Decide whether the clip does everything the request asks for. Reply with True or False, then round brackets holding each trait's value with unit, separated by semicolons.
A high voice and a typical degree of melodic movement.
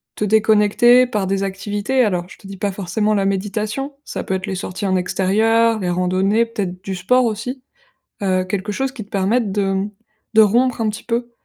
True (205 Hz; 3.0 semitones)